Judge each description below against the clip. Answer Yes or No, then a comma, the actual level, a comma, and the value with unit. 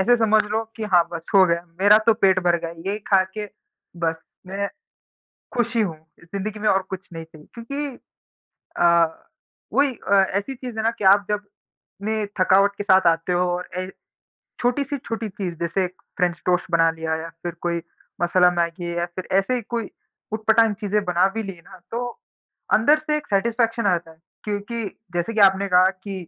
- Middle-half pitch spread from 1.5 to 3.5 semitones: No, average, 4.2 semitones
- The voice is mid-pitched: No, high, 195 Hz